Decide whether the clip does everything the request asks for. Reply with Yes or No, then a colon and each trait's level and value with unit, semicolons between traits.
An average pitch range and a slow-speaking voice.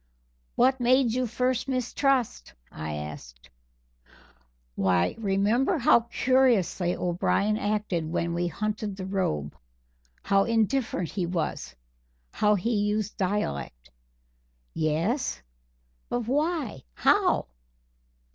No: wide, 6.1 semitones; slow, 100 wpm